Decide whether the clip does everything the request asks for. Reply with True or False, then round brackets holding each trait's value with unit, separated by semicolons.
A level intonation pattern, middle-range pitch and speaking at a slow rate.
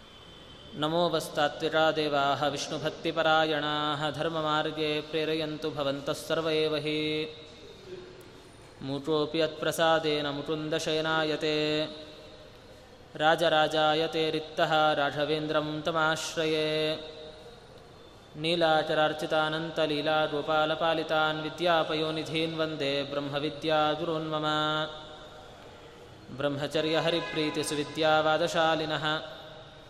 True (0.7 semitones; 155 Hz; 45 wpm)